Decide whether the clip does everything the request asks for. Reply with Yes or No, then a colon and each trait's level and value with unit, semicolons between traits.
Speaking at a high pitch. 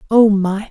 Yes: high, 205 Hz